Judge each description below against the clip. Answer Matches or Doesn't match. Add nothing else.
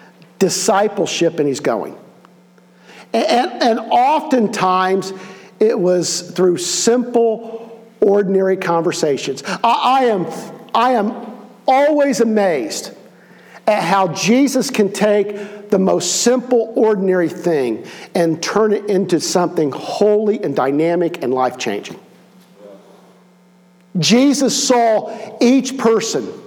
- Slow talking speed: Matches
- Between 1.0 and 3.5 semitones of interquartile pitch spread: Doesn't match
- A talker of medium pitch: Doesn't match